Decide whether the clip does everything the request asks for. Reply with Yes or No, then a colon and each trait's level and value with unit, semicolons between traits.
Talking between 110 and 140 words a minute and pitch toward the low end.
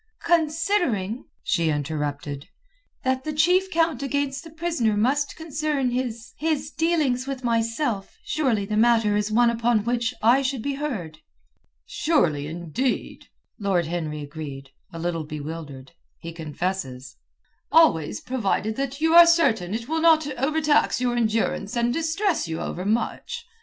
No: slow, 135 wpm; high, 235 Hz